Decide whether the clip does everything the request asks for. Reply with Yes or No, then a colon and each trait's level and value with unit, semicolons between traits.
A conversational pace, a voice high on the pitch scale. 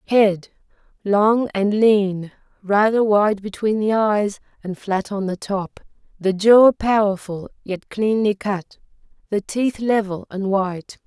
No: slow, 130 wpm; high, 205 Hz